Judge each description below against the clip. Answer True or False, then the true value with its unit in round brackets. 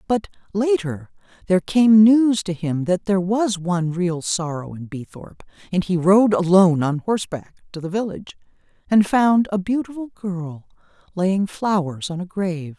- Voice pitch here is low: False (190 Hz)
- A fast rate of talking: False (160 wpm)